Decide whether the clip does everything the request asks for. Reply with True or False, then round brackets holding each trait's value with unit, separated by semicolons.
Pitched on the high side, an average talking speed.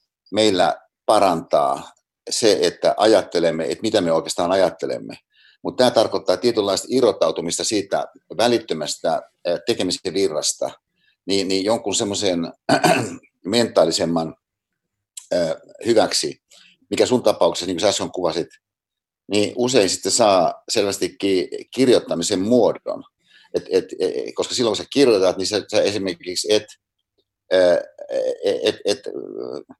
True (325 Hz; 115 wpm)